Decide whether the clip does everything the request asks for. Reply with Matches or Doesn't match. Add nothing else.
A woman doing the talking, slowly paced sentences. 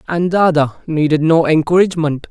Doesn't match